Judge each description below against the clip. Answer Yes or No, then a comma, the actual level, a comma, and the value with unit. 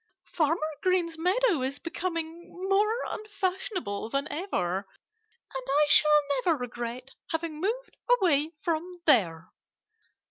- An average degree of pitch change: Yes, average, 5.0 semitones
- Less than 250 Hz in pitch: No, very high, 320 Hz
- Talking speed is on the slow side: Yes, slow, 110 wpm